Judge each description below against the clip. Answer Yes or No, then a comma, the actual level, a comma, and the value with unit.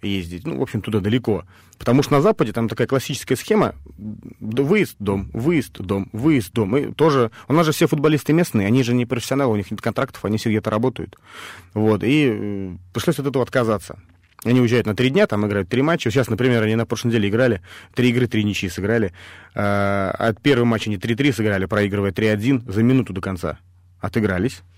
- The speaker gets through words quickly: Yes, fast, 195 wpm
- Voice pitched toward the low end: Yes, low, 110 Hz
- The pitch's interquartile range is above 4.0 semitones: Yes, average, 4.5 semitones